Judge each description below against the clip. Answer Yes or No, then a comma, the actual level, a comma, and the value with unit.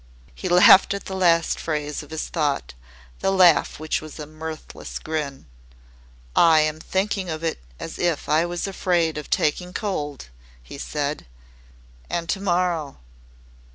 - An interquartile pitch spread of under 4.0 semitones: Yes, average, 2.9 semitones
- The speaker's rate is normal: Yes, average, 150 wpm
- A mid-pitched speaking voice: Yes, medium, 160 Hz